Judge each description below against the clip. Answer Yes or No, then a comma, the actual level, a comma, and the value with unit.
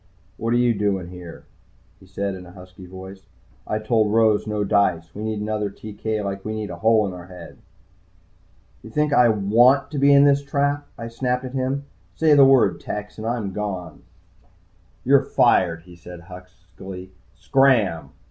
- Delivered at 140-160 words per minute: No, average, 175 wpm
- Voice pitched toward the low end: Yes, low, 105 Hz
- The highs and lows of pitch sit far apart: No, average, 4.7 semitones